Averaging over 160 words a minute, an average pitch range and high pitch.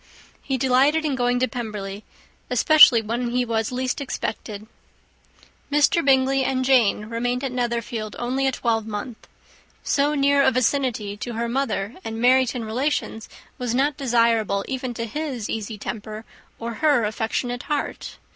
No: average, 145 wpm; average, 3.1 semitones; high, 245 Hz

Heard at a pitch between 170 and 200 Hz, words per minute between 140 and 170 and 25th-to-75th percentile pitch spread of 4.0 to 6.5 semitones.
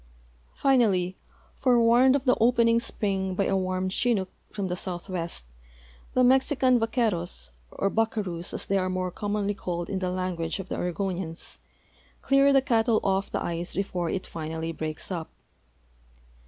Yes: high, 190 Hz; average, 150 wpm; average, 4.5 semitones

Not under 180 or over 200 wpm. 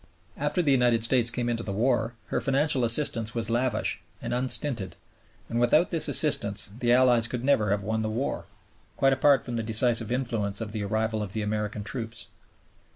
Yes: average, 185 wpm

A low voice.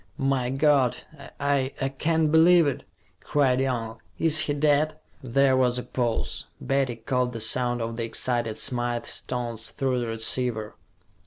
Yes: low, 130 Hz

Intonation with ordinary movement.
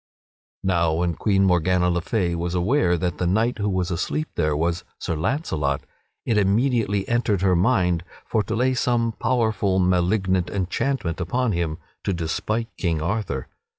Yes: average, 4.3 semitones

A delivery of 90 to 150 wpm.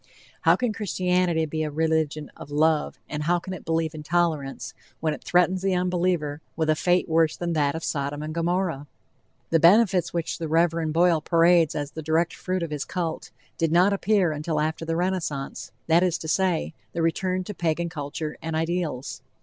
No: average, 190 wpm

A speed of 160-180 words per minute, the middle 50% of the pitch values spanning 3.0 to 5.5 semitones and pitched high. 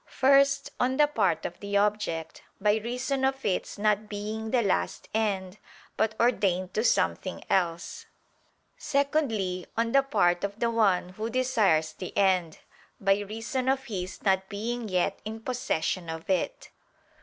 No: average, 150 wpm; average, 4.6 semitones; high, 210 Hz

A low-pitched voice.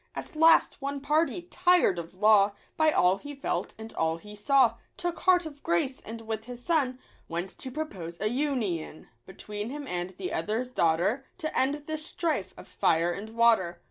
No: high, 235 Hz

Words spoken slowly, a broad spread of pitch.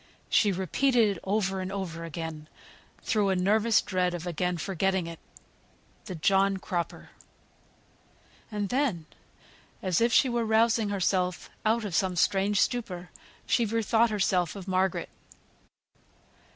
No: slow, 130 wpm; average, 3.3 semitones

